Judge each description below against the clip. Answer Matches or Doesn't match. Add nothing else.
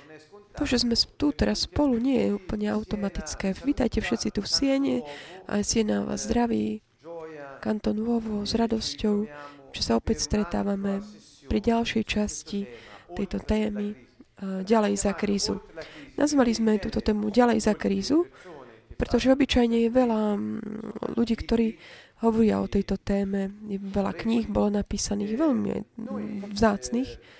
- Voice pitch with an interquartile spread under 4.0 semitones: Matches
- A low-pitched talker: Doesn't match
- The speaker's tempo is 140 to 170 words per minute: Doesn't match